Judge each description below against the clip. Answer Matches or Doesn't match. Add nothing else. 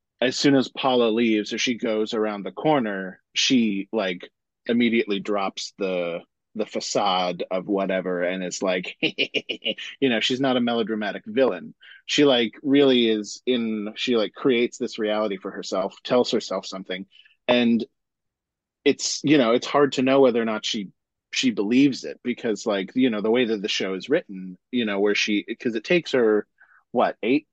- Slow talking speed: Doesn't match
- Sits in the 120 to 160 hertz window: Doesn't match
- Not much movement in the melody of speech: Doesn't match